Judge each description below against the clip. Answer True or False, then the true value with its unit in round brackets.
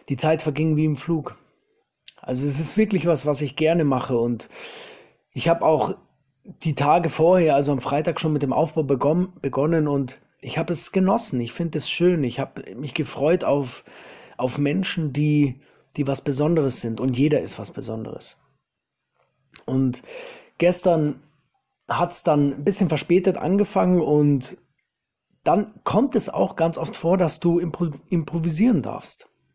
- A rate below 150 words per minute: False (160 wpm)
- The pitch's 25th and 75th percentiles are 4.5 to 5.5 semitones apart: False (3.8 semitones)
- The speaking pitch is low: False (155 Hz)